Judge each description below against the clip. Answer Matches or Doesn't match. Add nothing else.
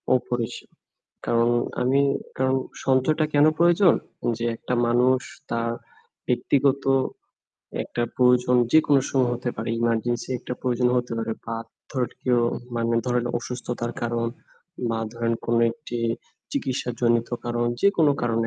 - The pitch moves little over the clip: Matches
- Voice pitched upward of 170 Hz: Doesn't match